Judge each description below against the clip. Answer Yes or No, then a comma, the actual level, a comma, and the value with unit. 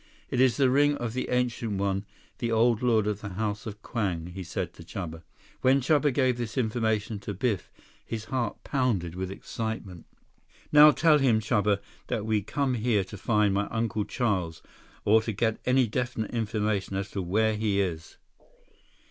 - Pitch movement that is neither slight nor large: Yes, average, 3.5 semitones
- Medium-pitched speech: No, low, 110 Hz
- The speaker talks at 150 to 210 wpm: Yes, average, 175 wpm